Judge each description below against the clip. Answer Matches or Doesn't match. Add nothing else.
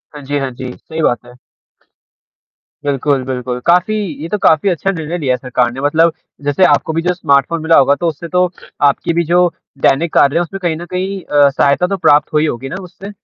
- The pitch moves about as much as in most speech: Matches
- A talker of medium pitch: Matches